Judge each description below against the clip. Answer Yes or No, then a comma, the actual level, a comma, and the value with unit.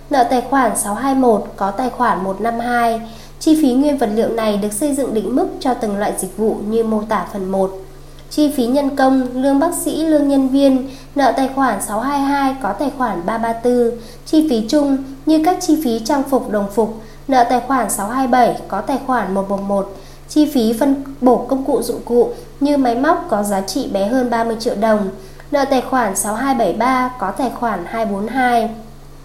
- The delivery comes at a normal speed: Yes, average, 190 wpm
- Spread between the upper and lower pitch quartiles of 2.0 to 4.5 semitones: Yes, average, 3.9 semitones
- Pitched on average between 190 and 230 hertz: No, high, 245 Hz